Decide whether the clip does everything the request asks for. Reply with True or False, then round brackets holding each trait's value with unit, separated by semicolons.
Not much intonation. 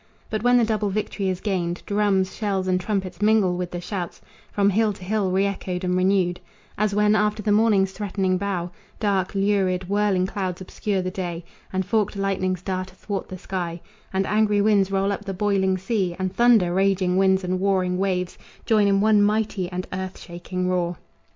True (2.1 semitones)